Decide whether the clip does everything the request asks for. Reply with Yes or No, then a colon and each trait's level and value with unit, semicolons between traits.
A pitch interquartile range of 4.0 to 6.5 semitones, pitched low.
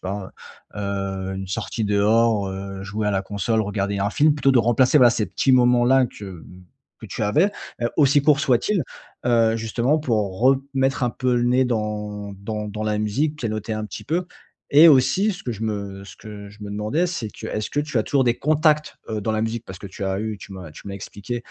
Yes: average, 4.4 semitones; low, 110 Hz